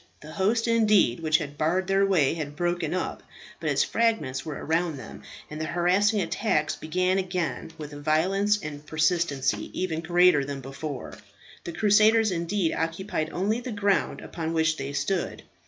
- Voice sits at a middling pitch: Yes, medium, 170 Hz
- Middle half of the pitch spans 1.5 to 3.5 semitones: No, average, 4.1 semitones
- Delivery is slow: No, average, 165 wpm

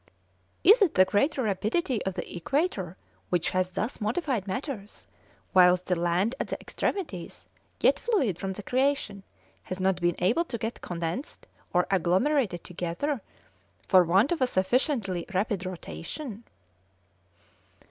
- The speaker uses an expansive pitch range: Yes, wide, 6.5 semitones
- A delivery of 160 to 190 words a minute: No, slow, 135 wpm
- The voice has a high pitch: Yes, high, 195 Hz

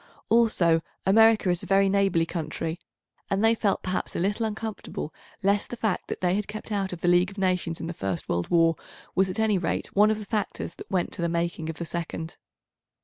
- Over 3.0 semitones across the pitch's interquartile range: Yes, average, 3.6 semitones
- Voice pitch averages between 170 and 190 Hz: Yes, medium, 185 Hz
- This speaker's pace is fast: Yes, fast, 215 wpm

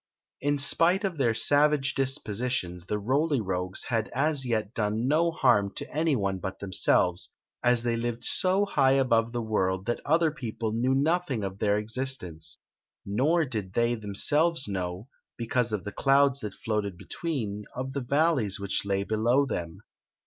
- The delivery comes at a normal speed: Yes, average, 165 wpm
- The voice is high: No, low, 120 Hz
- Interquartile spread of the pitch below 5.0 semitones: No, wide, 5.5 semitones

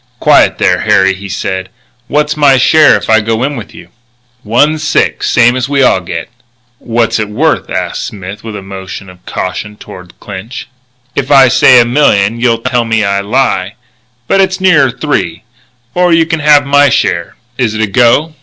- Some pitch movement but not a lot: No, wide, 6.2 semitones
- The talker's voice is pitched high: No, low, 115 Hz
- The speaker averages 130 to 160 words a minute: No, average, 180 wpm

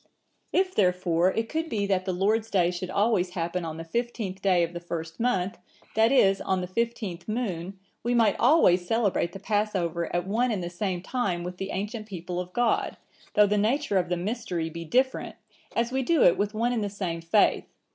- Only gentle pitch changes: No, average, 4.2 semitones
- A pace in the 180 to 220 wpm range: Yes, fast, 205 wpm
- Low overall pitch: No, high, 195 Hz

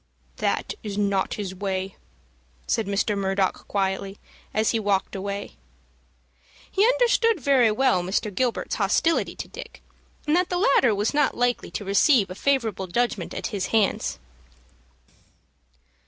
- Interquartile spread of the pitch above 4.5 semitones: Yes, average, 5.1 semitones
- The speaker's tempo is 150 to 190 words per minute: No, average, 140 wpm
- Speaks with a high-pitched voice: Yes, high, 210 Hz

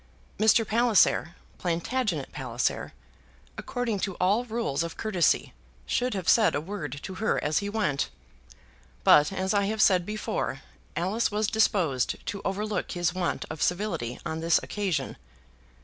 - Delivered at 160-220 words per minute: No, average, 145 wpm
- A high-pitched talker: Yes, high, 195 Hz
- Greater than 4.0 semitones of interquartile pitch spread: Yes, average, 4.5 semitones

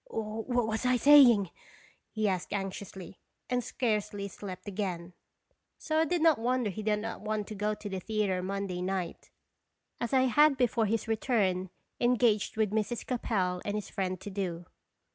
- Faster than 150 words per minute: Yes, average, 165 wpm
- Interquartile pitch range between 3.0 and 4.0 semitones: Yes, average, 3.7 semitones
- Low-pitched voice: No, high, 210 Hz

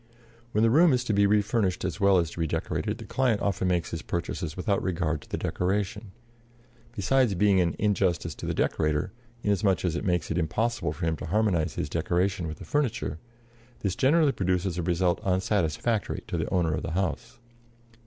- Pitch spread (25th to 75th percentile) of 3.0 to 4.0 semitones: Yes, average, 3.7 semitones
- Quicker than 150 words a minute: Yes, average, 185 wpm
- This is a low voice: Yes, very low, 95 Hz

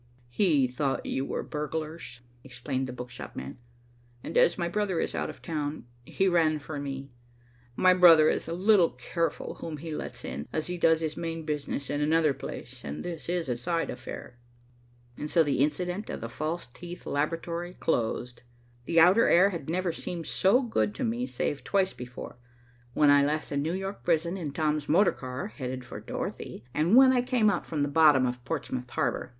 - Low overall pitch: No, medium, 155 Hz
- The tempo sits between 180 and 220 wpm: Yes, average, 195 wpm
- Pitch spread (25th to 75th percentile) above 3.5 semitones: Yes, average, 4.3 semitones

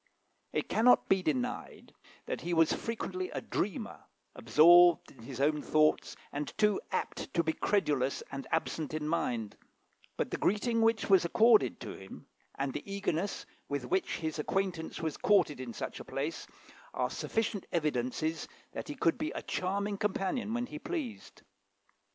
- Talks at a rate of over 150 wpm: Yes, average, 160 wpm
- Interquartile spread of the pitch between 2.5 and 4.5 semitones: No, wide, 5.6 semitones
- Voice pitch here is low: No, medium, 170 Hz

